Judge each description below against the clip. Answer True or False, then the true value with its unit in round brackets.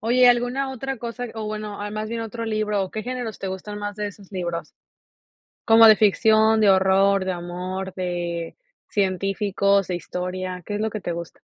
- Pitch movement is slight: False (3.0 semitones)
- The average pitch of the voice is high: True (205 Hz)